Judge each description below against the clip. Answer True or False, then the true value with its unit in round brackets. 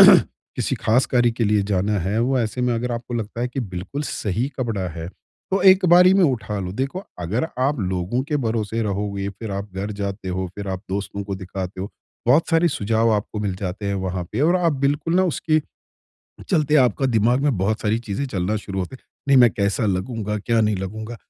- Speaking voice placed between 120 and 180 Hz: False (110 Hz)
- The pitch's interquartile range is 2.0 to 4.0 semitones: False (4.6 semitones)